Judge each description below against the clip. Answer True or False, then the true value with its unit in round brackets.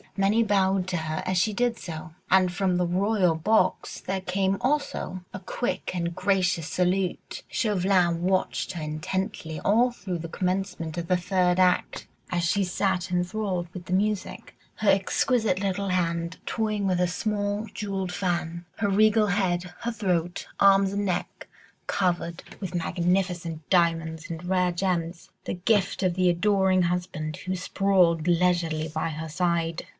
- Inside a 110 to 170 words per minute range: True (155 wpm)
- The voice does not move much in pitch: True (2.3 semitones)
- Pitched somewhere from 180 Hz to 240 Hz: True (185 Hz)